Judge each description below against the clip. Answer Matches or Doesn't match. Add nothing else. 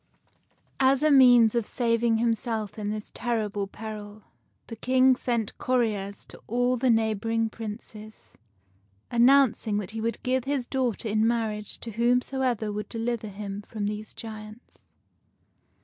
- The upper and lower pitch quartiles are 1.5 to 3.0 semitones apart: Matches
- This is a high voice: Matches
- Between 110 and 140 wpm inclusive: Matches